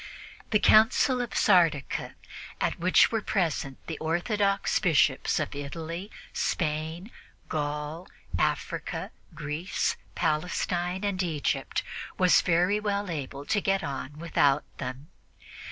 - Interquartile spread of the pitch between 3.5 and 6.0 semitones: Yes, average, 4.6 semitones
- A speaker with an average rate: No, slow, 110 wpm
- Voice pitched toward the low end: No, medium, 170 Hz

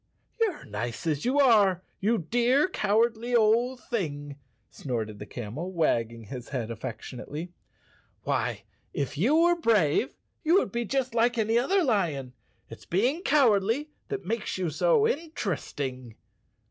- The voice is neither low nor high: No, high, 210 Hz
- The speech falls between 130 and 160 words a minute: Yes, average, 145 wpm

